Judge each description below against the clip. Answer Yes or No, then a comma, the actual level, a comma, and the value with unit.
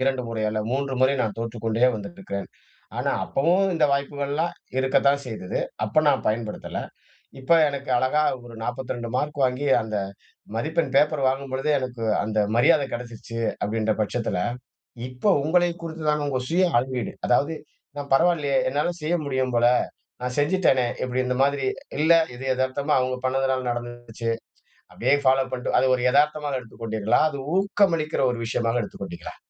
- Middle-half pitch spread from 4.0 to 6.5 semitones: No, average, 3.5 semitones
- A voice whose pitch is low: Yes, low, 130 Hz